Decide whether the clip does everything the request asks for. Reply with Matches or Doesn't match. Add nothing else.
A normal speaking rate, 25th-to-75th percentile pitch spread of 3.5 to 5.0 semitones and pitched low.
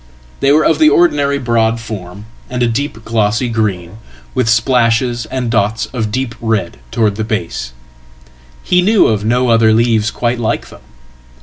Doesn't match